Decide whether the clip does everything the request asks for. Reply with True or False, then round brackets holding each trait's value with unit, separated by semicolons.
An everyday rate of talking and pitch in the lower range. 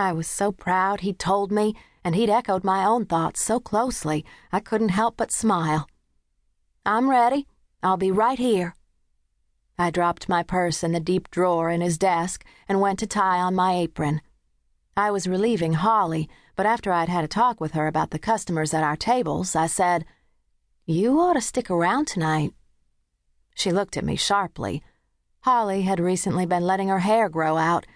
False (180 wpm; 185 Hz)